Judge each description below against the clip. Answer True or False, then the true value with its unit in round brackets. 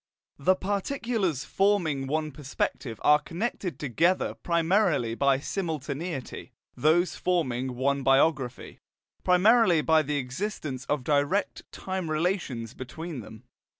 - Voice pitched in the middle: True (155 Hz)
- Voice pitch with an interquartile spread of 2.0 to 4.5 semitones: False (5.2 semitones)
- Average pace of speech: False (110 wpm)